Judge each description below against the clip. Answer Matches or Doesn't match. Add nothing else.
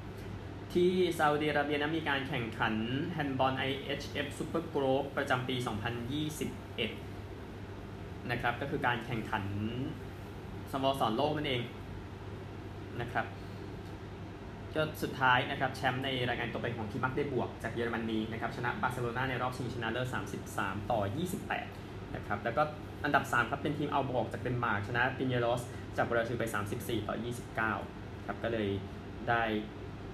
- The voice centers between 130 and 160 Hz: Doesn't match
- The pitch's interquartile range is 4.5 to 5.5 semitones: Matches